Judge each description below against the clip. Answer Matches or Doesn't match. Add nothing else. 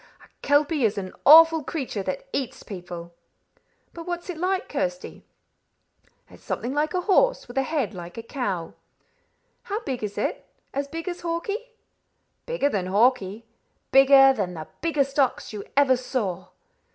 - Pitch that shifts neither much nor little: Doesn't match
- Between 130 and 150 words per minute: Doesn't match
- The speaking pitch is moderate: Doesn't match